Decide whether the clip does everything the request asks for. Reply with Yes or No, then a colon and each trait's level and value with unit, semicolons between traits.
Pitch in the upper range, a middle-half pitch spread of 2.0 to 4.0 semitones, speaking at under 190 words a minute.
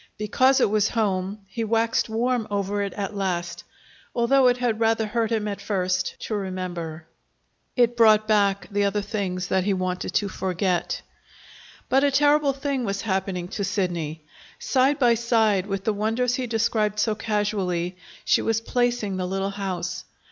Yes: high, 210 Hz; average, 3.3 semitones; average, 165 wpm